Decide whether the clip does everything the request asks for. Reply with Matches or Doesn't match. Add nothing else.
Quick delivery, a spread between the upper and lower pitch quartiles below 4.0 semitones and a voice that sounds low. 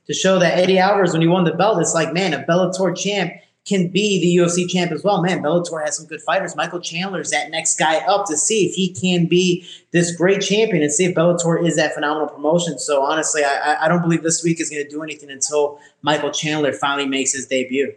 Doesn't match